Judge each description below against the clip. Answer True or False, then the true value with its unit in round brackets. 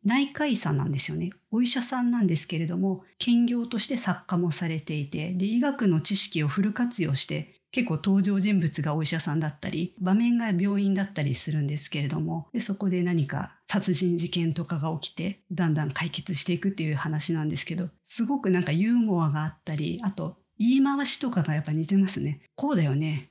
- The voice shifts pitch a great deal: False (4.1 semitones)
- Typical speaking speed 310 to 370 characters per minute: False (410 characters per minute)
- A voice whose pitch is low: False (175 Hz)